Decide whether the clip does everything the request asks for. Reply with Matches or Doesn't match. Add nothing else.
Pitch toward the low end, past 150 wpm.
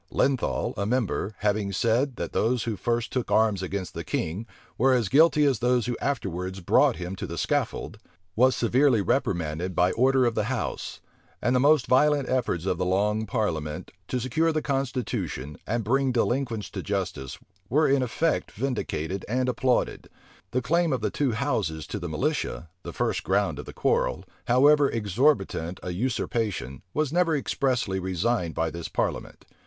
Matches